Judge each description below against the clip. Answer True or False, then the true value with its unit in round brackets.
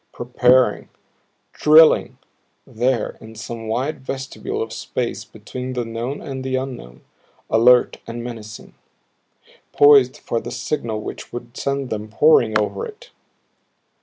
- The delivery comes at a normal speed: False (125 wpm)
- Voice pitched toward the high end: False (120 Hz)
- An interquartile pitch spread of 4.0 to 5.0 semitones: False (2.9 semitones)